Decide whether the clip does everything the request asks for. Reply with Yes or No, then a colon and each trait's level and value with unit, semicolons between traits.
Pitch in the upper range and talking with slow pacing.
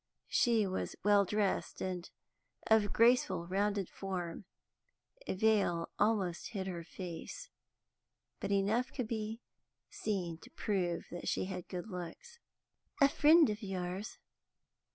Yes: high, 200 Hz; slow, 130 wpm